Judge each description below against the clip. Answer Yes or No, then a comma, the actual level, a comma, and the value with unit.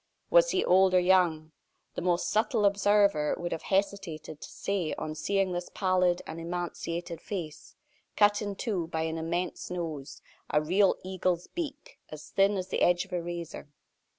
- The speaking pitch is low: No, medium, 180 Hz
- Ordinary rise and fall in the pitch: Yes, average, 3.2 semitones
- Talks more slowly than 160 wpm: No, average, 170 wpm